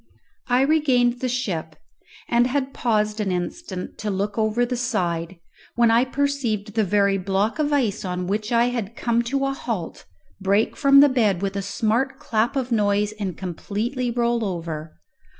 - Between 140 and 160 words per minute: No, average, 170 wpm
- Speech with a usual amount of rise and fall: Yes, average, 4.0 semitones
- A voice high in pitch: Yes, high, 225 Hz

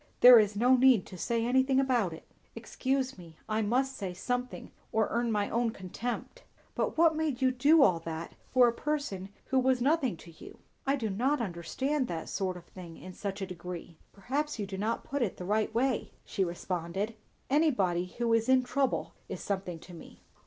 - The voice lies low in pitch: No, high, 230 Hz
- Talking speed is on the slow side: No, average, 195 wpm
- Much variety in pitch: Yes, wide, 5.9 semitones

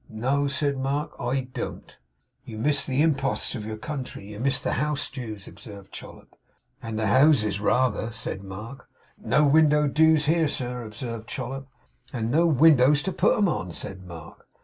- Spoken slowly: No, average, 170 wpm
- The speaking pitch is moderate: No, low, 130 Hz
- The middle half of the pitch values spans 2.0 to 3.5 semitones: No, average, 5.1 semitones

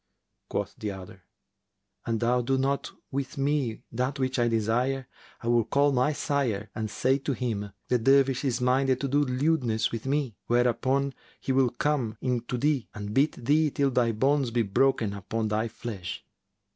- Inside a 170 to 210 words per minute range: Yes, average, 175 wpm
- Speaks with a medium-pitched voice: No, low, 125 Hz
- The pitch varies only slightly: No, average, 3.3 semitones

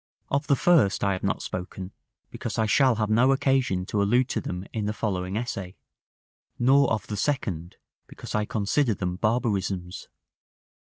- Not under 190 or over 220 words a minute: No, average, 165 wpm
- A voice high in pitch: No, low, 105 Hz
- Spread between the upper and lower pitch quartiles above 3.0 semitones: Yes, average, 5.1 semitones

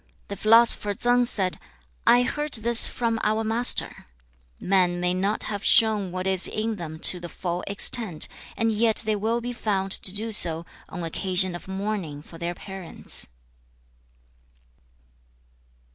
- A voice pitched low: No, high, 200 Hz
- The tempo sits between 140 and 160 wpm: Yes, average, 145 wpm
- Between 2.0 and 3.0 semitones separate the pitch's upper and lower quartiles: No, average, 3.8 semitones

